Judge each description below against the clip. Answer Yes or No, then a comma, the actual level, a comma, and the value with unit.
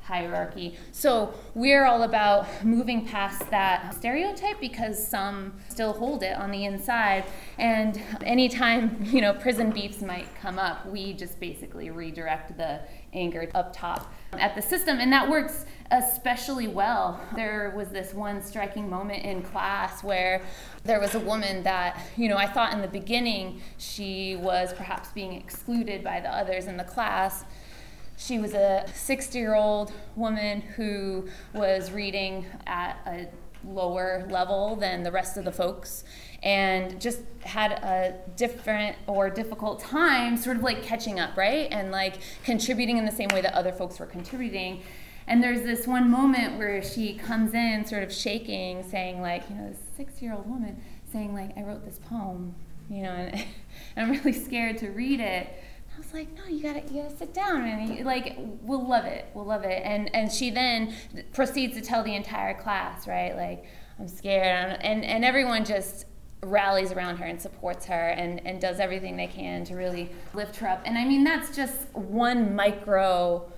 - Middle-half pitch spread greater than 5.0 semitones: No, average, 3.9 semitones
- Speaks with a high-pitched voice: Yes, high, 205 Hz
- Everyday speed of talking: Yes, average, 175 wpm